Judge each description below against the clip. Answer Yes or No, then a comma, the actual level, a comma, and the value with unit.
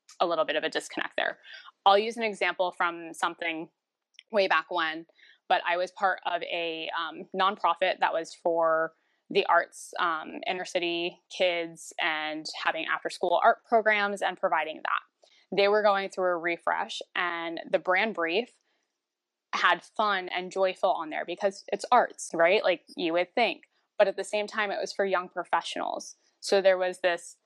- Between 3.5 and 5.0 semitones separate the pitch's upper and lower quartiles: No, average, 2.7 semitones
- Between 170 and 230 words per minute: Yes, average, 175 wpm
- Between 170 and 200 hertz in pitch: Yes, medium, 185 Hz